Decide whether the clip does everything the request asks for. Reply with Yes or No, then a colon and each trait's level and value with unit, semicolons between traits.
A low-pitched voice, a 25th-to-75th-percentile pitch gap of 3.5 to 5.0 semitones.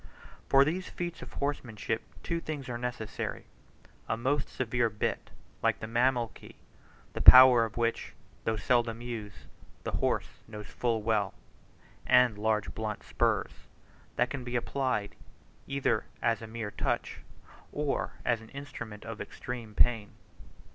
No: low, 120 Hz; average, 2.8 semitones